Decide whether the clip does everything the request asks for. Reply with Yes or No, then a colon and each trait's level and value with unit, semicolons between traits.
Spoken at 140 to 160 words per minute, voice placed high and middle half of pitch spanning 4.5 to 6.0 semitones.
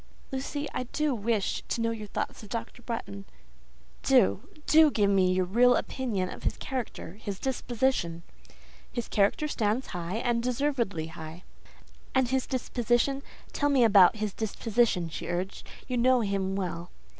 Yes: average, 155 wpm; high, 225 Hz; average, 5.0 semitones